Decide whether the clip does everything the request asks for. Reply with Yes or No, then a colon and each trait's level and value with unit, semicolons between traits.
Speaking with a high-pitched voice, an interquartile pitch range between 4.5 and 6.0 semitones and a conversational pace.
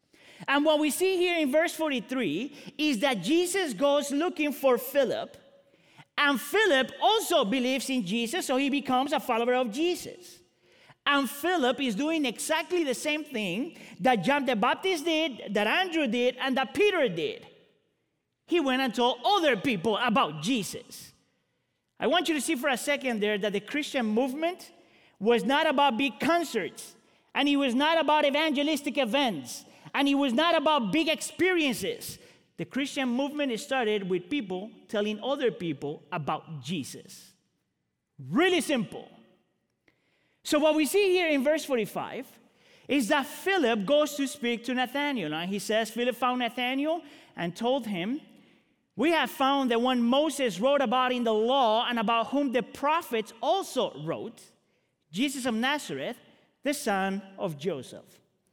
No: very high, 270 Hz; average, 4.1 semitones; average, 155 wpm